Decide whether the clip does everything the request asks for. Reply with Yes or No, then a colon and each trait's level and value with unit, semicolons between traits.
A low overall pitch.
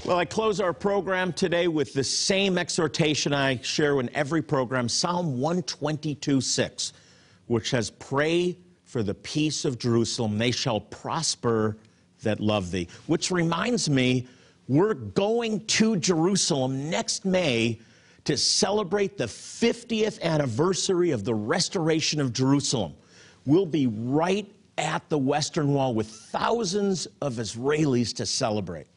No: medium, 145 Hz